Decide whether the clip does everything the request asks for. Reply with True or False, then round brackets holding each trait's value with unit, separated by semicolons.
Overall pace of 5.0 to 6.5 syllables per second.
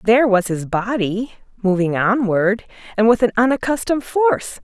True (5.2 syllables/s)